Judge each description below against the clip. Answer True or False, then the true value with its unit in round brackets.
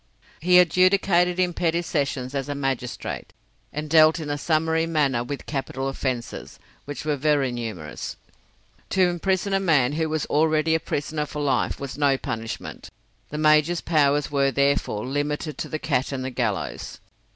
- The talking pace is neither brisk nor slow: True (160 wpm)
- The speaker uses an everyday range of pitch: True (3.1 semitones)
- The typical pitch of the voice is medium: True (150 Hz)